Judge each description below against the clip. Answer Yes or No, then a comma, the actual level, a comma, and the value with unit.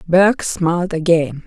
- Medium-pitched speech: Yes, medium, 175 Hz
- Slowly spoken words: Yes, slow, 125 wpm